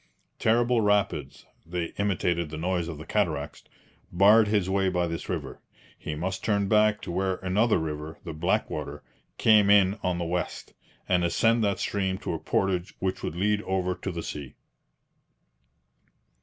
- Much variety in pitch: No, average, 3.2 semitones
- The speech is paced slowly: No, average, 160 wpm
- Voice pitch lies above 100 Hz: No, very low, 95 Hz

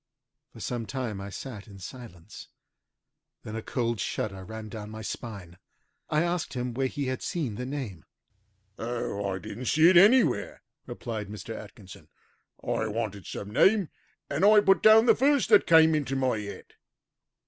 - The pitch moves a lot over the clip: Yes, wide, 6.5 semitones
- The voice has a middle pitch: No, low, 120 Hz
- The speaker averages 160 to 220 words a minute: Yes, average, 165 wpm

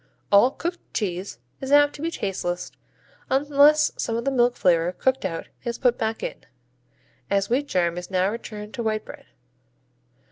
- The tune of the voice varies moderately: No, wide, 6.0 semitones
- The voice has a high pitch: Yes, high, 225 Hz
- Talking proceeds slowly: No, average, 170 wpm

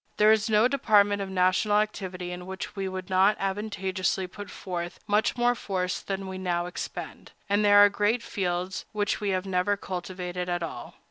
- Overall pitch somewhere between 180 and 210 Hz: Yes, high, 190 Hz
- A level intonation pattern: Yes, narrow, 2.2 semitones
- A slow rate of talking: No, average, 185 wpm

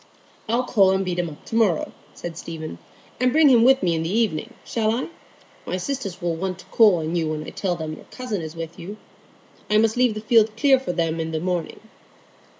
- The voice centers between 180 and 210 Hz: Yes, high, 190 Hz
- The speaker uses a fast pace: Yes, fast, 230 wpm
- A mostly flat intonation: No, wide, 5.6 semitones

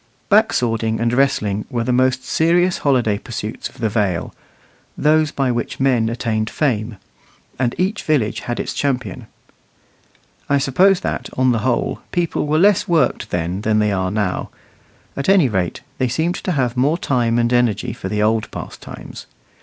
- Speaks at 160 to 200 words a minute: Yes, average, 170 wpm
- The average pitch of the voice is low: Yes, low, 125 Hz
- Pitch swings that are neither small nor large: Yes, average, 4.7 semitones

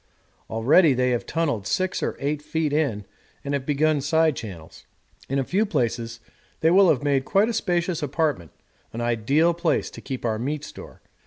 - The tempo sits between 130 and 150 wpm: No, average, 180 wpm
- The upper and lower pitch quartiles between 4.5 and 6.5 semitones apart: Yes, average, 5.1 semitones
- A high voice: No, medium, 145 Hz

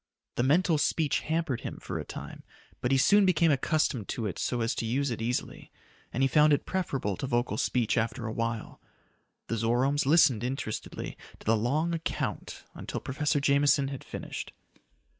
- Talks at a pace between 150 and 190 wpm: Yes, average, 180 wpm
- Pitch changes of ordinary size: Yes, average, 4.3 semitones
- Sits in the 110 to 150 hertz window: Yes, low, 135 Hz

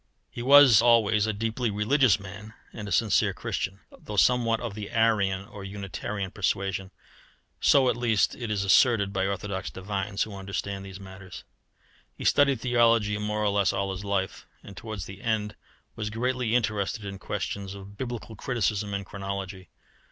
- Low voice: Yes, low, 105 Hz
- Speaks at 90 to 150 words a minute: No, average, 165 wpm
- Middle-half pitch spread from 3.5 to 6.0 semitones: No, narrow, 2.5 semitones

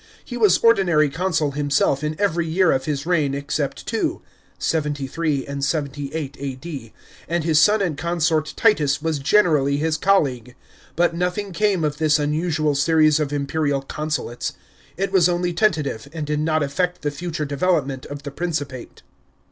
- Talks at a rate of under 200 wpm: Yes, average, 155 wpm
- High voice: No, medium, 155 Hz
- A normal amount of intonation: Yes, average, 3.4 semitones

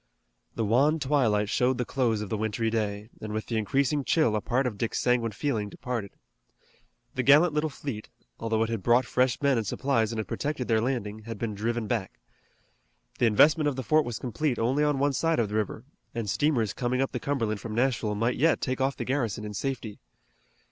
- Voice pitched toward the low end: Yes, low, 120 Hz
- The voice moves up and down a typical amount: Yes, average, 3.8 semitones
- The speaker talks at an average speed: No, fast, 210 wpm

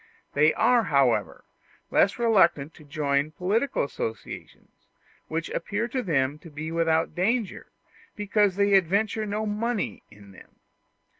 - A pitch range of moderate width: No, wide, 5.8 semitones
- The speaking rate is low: Yes, slow, 130 wpm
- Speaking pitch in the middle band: Yes, medium, 180 Hz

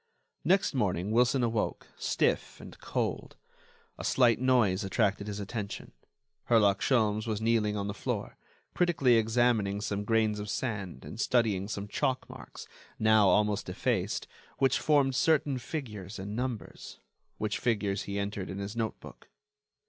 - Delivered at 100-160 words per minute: Yes, average, 140 wpm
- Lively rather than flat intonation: No, average, 3.2 semitones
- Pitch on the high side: No, low, 110 Hz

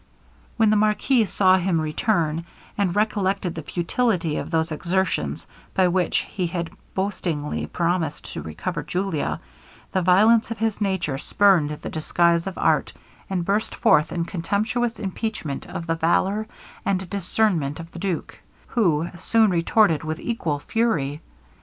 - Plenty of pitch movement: No, average, 3.9 semitones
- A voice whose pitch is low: No, medium, 180 Hz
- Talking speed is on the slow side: No, average, 145 wpm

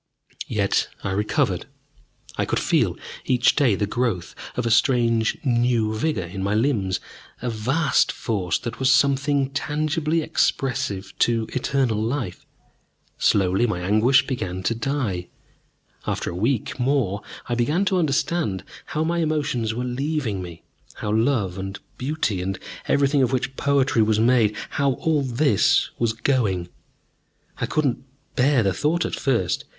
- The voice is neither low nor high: No, low, 120 Hz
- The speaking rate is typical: Yes, average, 145 wpm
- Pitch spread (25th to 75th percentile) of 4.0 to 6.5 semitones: Yes, average, 5.0 semitones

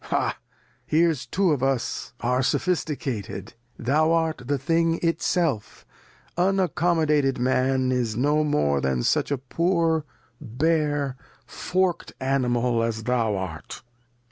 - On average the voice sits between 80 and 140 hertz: Yes, low, 135 Hz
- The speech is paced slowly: Yes, slow, 115 wpm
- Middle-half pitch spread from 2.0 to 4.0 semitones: No, average, 5.1 semitones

